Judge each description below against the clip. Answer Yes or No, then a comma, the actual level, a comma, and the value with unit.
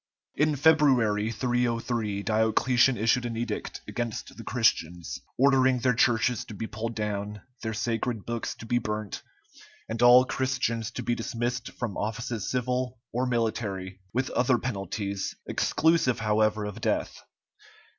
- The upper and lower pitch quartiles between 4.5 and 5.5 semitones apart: No, narrow, 2.6 semitones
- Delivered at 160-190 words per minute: No, slow, 135 wpm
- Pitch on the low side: Yes, low, 115 Hz